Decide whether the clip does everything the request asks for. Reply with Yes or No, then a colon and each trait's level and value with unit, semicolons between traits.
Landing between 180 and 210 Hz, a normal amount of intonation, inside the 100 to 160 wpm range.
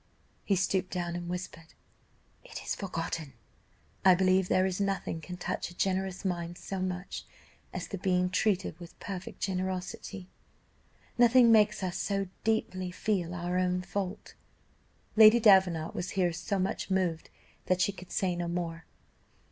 No: medium, 185 Hz; narrow, 1.7 semitones; average, 150 wpm